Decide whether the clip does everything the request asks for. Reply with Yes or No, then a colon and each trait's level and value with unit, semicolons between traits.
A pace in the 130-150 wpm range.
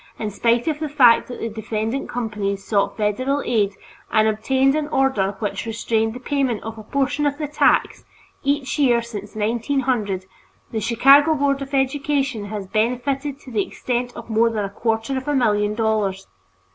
No: average, 175 wpm